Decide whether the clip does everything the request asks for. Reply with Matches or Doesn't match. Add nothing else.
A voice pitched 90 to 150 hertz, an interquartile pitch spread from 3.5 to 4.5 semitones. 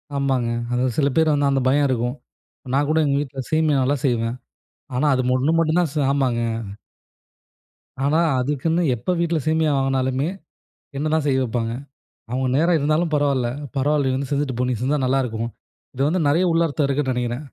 Doesn't match